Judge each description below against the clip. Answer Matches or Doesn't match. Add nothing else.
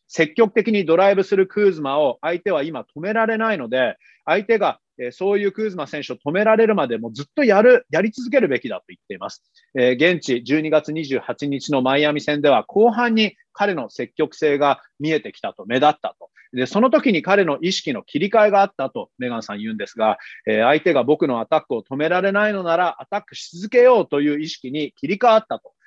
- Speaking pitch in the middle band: Matches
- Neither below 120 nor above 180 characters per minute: Doesn't match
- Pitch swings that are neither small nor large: Doesn't match